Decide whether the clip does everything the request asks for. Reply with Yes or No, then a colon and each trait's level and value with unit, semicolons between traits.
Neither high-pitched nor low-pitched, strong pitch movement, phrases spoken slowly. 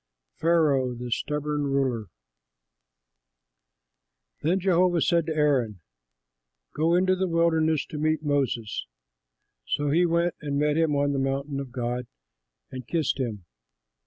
No: medium, 150 Hz; average, 3.6 semitones; slow, 130 wpm